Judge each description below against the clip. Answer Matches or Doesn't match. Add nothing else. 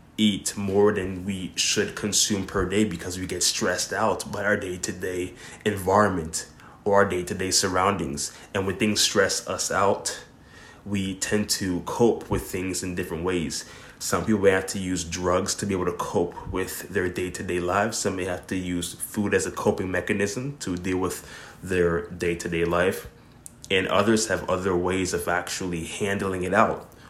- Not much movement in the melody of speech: Matches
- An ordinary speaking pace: Matches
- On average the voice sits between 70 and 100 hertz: Matches